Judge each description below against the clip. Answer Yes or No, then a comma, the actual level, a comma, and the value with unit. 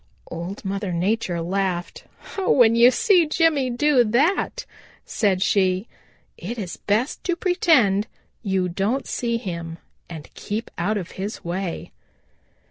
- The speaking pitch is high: Yes, high, 205 Hz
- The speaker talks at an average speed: No, slow, 130 wpm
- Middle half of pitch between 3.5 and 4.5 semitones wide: No, average, 5.2 semitones